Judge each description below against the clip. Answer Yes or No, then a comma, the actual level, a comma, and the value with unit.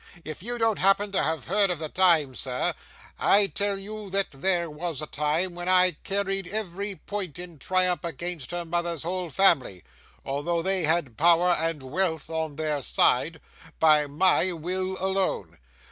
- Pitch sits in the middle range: Yes, medium, 175 Hz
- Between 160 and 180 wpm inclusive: Yes, average, 165 wpm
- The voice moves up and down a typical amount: Yes, average, 3.6 semitones